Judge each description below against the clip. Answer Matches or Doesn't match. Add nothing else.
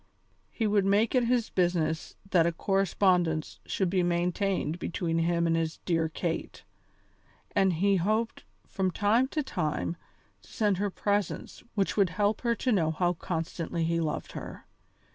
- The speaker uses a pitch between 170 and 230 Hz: Matches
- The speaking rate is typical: Matches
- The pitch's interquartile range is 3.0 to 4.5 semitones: Matches